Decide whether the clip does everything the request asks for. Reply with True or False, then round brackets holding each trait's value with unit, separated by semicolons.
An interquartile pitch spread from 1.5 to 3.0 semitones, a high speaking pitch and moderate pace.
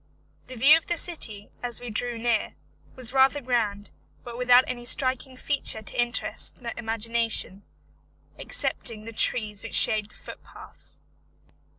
True (2.6 semitones; 240 Hz; 145 wpm)